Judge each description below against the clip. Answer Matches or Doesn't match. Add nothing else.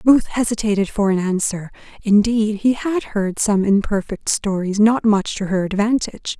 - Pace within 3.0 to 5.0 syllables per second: Matches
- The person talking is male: Doesn't match